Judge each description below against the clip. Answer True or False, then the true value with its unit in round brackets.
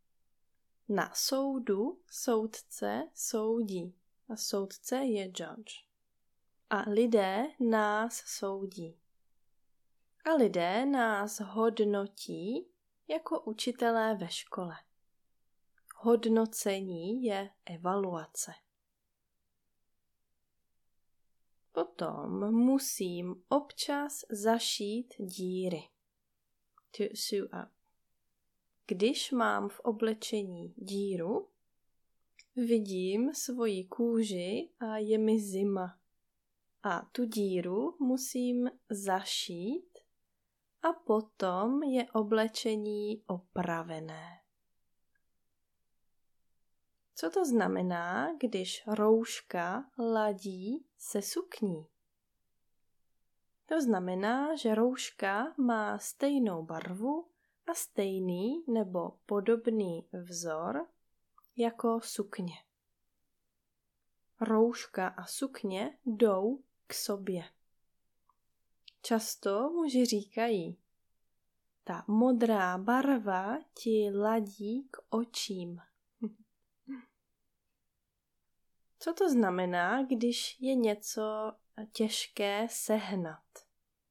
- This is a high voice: True (220 Hz)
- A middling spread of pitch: True (4.2 semitones)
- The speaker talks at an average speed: False (70 wpm)